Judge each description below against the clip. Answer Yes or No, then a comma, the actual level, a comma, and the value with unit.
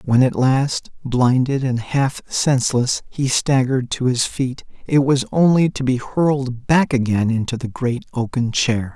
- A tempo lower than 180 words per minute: Yes, average, 170 wpm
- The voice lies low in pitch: Yes, low, 130 Hz